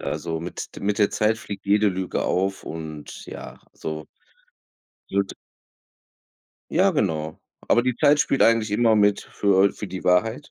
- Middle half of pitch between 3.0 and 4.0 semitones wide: Yes, average, 3.7 semitones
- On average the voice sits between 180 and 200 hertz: No, low, 100 Hz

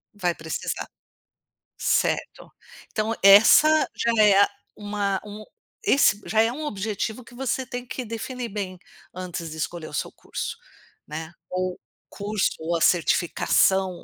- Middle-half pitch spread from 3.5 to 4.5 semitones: Yes, average, 3.8 semitones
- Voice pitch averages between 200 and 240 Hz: Yes, high, 205 Hz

